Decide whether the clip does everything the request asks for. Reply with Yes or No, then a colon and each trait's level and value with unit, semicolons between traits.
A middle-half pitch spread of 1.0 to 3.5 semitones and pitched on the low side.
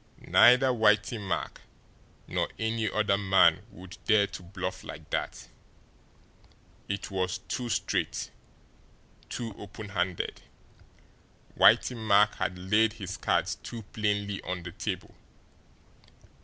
Yes: average, 2.7 semitones; low, 100 Hz